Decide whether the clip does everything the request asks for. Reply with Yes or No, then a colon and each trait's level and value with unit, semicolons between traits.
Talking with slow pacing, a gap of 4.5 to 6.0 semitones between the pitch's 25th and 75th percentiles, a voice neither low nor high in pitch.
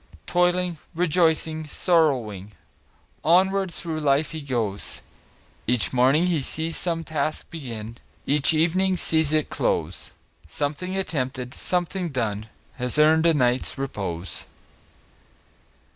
Yes: slow, 105 wpm; average, 4.9 semitones; medium, 155 Hz